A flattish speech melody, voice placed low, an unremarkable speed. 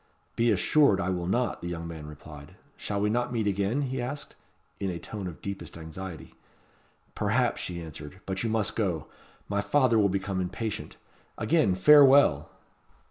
No: average, 4.8 semitones; low, 100 Hz; average, 165 wpm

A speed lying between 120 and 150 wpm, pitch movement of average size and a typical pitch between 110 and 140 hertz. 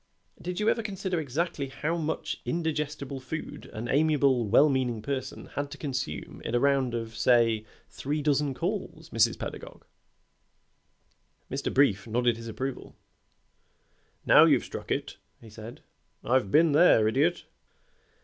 Yes: average, 140 wpm; average, 4.7 semitones; low, 135 Hz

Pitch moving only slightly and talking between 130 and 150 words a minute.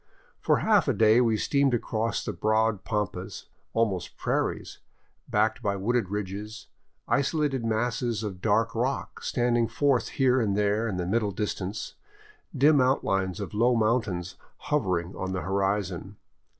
No: average, 3.4 semitones; slow, 135 wpm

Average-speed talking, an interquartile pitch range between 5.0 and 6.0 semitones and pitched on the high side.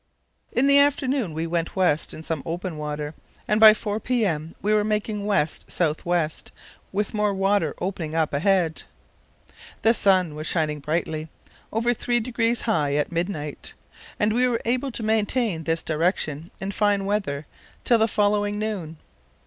Yes: average, 160 wpm; average, 5.3 semitones; high, 195 Hz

